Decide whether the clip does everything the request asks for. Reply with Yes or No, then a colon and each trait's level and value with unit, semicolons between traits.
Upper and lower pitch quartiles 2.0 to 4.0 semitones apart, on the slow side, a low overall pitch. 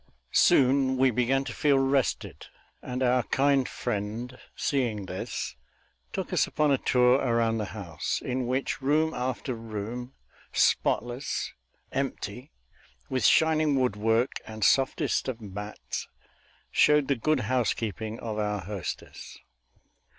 Yes: average, 3.6 semitones; slow, 120 wpm; low, 125 Hz